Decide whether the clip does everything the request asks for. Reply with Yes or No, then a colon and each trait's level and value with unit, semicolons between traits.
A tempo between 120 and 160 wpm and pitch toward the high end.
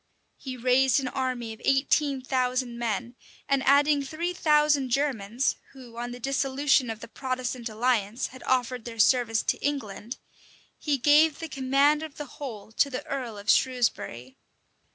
Yes: average, 155 wpm; very high, 255 Hz